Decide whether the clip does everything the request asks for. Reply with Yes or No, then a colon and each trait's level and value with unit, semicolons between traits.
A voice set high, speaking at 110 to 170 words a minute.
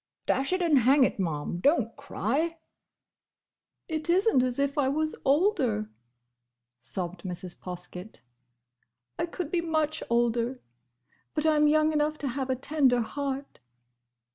Yes: very high, 275 Hz; average, 140 wpm